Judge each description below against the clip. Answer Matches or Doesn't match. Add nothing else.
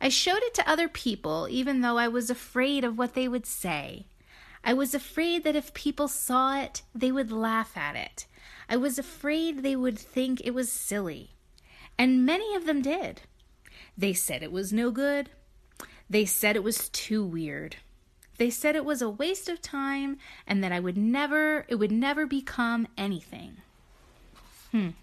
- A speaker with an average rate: Matches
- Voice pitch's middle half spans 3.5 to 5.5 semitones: Matches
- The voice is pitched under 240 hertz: Doesn't match